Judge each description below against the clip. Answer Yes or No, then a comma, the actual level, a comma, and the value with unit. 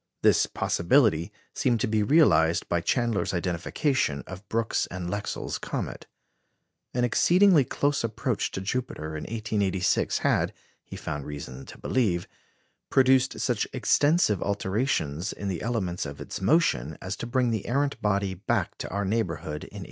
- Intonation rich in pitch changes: Yes, wide, 6.3 semitones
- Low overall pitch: Yes, low, 105 Hz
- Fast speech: No, average, 150 wpm